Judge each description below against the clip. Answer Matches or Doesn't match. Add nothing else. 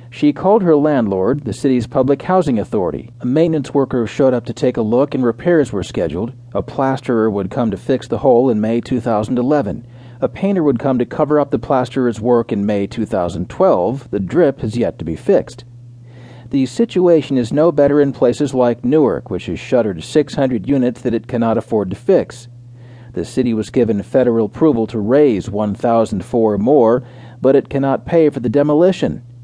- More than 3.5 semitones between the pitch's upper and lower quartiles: Doesn't match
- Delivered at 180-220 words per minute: Matches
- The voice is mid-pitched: Doesn't match